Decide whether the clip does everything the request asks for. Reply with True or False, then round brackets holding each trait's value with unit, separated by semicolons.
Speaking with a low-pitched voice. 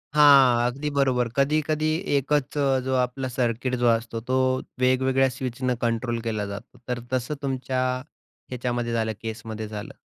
True (125 Hz)